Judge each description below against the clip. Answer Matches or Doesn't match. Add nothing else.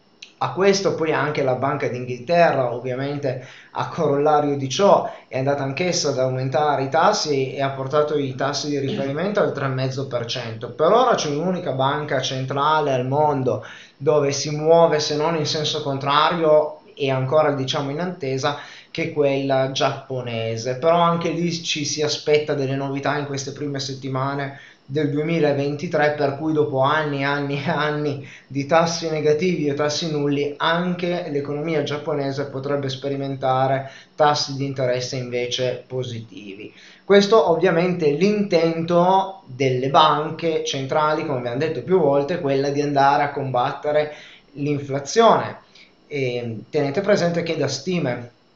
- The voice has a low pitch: Doesn't match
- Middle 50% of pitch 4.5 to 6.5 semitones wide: Doesn't match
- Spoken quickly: Doesn't match